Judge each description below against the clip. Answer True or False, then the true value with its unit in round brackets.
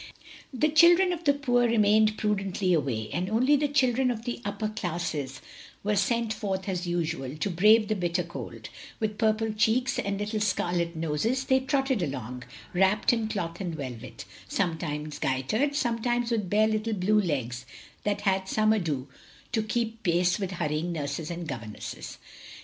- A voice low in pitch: False (205 Hz)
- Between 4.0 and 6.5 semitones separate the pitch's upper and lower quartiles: True (5.2 semitones)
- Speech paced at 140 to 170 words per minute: True (160 wpm)